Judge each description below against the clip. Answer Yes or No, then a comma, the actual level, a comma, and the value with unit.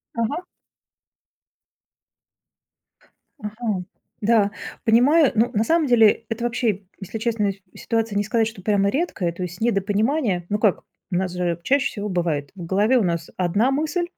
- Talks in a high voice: Yes, high, 215 Hz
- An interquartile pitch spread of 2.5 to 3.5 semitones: No, average, 4.1 semitones